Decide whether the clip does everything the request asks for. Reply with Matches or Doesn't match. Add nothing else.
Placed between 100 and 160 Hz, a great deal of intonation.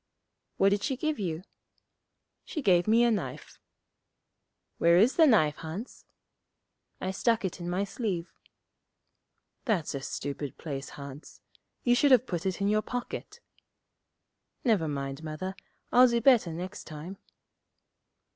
Doesn't match